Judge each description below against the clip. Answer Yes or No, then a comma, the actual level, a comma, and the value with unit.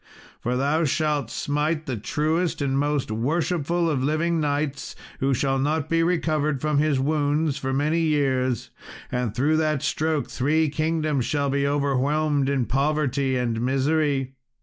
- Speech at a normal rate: Yes, average, 150 wpm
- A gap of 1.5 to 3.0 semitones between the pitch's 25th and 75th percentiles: Yes, narrow, 2.5 semitones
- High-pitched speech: No, medium, 145 Hz